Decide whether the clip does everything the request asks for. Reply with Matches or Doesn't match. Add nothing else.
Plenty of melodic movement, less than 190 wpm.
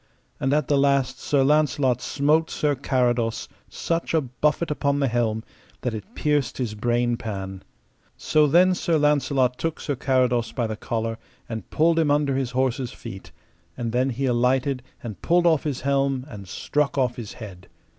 Doesn't match